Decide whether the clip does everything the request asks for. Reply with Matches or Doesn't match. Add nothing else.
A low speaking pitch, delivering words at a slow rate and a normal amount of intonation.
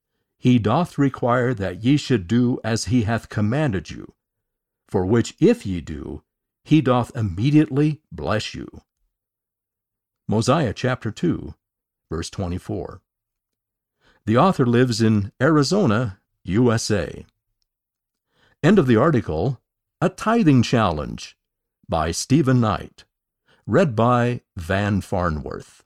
Matches